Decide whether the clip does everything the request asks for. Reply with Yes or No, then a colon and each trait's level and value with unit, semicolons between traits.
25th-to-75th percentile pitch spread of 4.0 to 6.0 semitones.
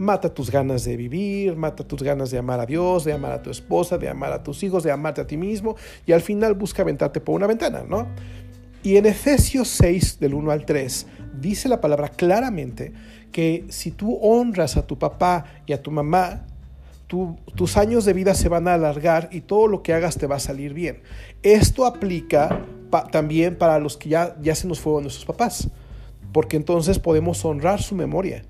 Yes: average, 4.5 semitones